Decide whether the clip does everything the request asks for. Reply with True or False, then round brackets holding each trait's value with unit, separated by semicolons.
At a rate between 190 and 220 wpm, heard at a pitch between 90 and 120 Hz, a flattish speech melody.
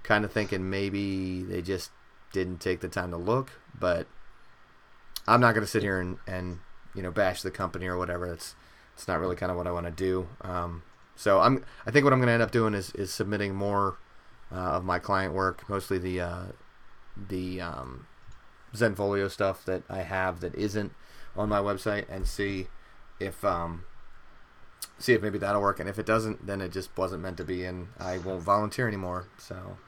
True (205 wpm; 95 Hz; 1.9 semitones)